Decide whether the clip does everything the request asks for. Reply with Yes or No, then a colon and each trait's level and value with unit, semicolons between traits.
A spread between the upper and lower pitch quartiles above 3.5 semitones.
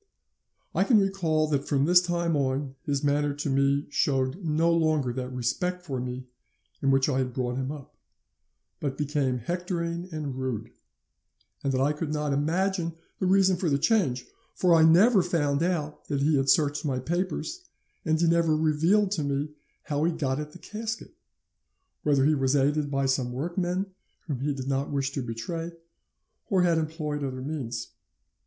Yes: average, 3.9 semitones